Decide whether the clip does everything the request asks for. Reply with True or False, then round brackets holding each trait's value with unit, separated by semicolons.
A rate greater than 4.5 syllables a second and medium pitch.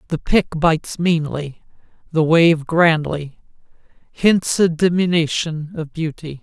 False (4.1 syllables/s; 160 Hz)